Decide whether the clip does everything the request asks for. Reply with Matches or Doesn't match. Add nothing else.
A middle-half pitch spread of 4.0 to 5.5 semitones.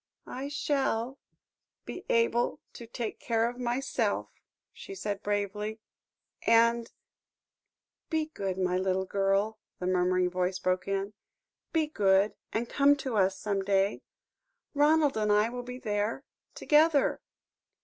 Matches